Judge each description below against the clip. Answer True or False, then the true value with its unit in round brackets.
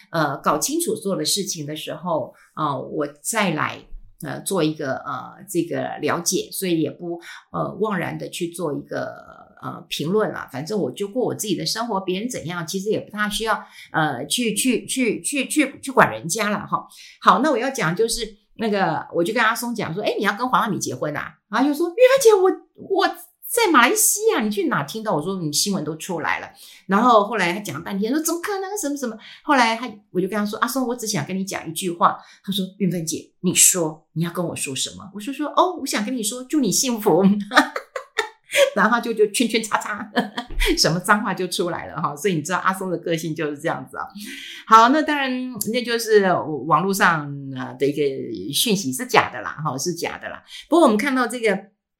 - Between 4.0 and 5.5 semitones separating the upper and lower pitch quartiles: False (6.3 semitones)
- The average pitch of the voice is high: True (210 Hz)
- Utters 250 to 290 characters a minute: False (300 characters per minute)